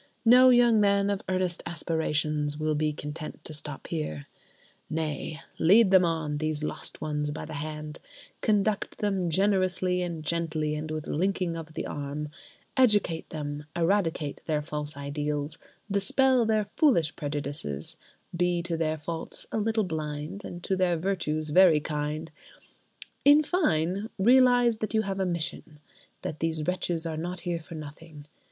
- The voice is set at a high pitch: No, medium, 165 Hz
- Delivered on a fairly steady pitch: No, average, 4.1 semitones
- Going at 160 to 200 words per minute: No, average, 150 wpm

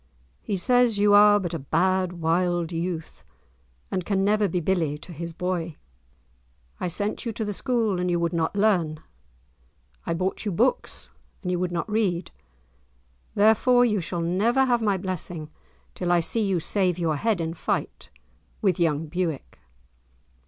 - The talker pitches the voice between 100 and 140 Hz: No, medium, 180 Hz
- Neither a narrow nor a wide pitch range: Yes, average, 3.5 semitones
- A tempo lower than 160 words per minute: No, average, 165 wpm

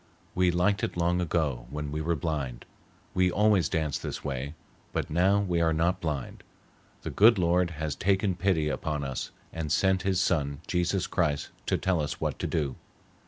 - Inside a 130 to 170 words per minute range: No, average, 180 wpm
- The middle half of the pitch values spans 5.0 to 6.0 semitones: No, average, 3.6 semitones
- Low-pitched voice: Yes, very low, 85 Hz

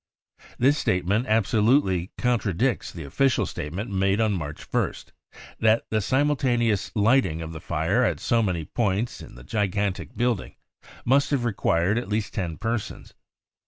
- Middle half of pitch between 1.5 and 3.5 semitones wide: No, average, 4.6 semitones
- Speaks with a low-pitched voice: Yes, low, 105 Hz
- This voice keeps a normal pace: Yes, average, 150 wpm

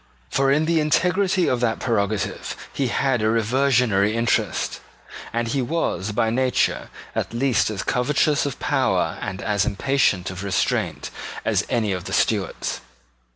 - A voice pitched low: Yes, low, 120 Hz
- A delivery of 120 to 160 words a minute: Yes, average, 150 wpm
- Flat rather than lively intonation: No, average, 4.8 semitones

